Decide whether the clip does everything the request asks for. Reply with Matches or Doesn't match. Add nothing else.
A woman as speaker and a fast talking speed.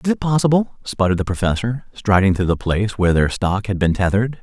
Doesn't match